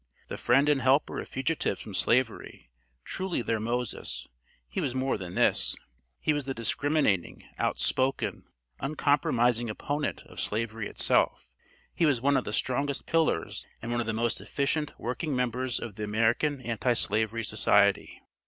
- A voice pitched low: Yes, low, 125 Hz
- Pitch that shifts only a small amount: No, average, 3.9 semitones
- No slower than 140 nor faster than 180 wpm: Yes, average, 155 wpm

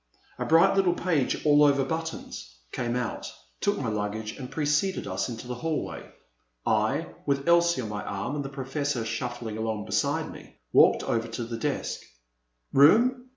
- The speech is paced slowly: No, average, 165 wpm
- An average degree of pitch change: No, wide, 5.8 semitones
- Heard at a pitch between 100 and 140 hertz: Yes, low, 135 Hz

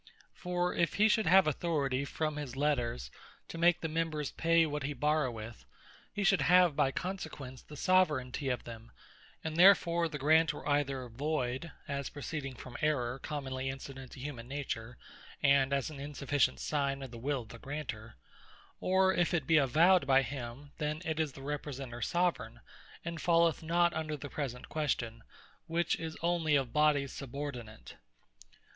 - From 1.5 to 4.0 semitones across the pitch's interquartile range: Yes, average, 3.7 semitones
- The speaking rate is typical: Yes, average, 160 wpm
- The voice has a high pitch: No, medium, 145 Hz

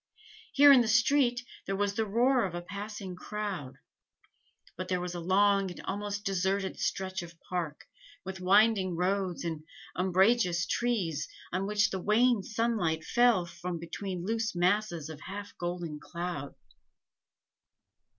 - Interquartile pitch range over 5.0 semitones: No, average, 3.3 semitones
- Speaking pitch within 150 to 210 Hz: Yes, high, 190 Hz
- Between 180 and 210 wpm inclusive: No, average, 140 wpm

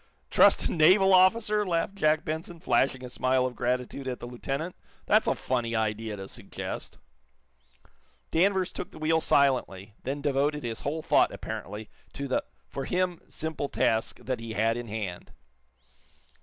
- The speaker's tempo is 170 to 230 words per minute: No, average, 155 wpm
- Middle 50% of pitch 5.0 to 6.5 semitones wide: Yes, wide, 5.4 semitones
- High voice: No, low, 135 Hz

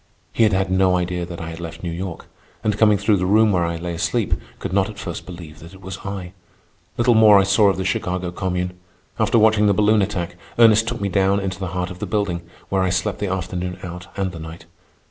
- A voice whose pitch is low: Yes, very low, 95 Hz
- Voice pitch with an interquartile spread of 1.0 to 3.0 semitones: Yes, narrow, 2.5 semitones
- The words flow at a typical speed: No, fast, 240 wpm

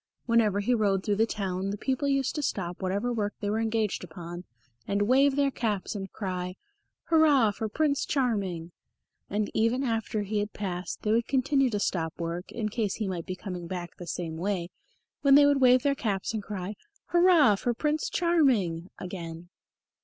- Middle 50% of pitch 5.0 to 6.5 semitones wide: Yes, wide, 5.4 semitones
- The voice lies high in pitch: Yes, high, 210 Hz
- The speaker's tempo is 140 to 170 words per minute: No, average, 185 wpm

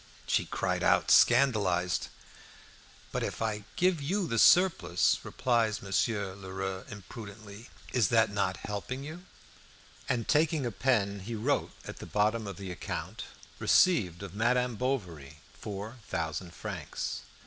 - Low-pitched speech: Yes, low, 105 Hz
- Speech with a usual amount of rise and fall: Yes, average, 4.5 semitones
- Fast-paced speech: No, slow, 135 wpm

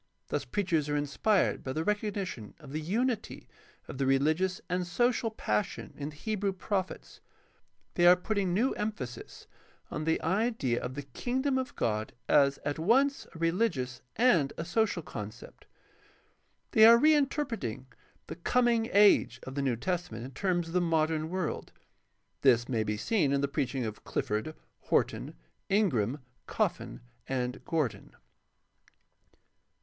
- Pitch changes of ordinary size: No, wide, 7.7 semitones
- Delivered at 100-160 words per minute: Yes, average, 145 wpm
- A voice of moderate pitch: Yes, medium, 165 Hz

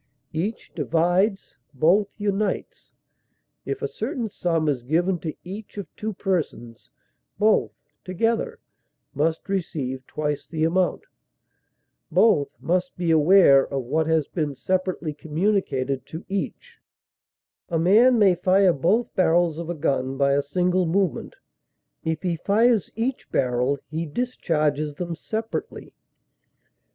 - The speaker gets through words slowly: Yes, slow, 125 wpm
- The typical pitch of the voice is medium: Yes, medium, 175 Hz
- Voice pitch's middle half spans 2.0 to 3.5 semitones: No, average, 4.7 semitones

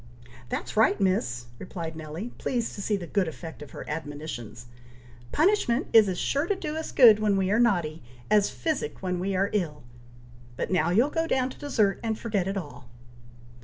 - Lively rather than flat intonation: Yes, wide, 6.3 semitones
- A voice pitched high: Yes, high, 195 Hz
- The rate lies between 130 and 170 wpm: No, average, 190 wpm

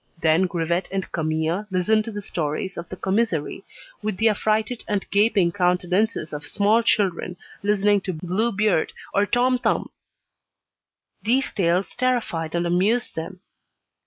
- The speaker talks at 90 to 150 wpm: Yes, average, 140 wpm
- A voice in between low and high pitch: No, high, 195 Hz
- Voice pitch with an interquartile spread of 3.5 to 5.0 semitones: Yes, average, 3.8 semitones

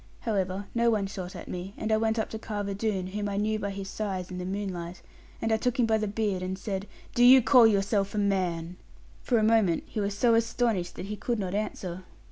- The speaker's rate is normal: No, fast, 240 wpm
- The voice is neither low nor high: No, high, 205 Hz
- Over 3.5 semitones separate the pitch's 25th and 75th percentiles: No, average, 2.7 semitones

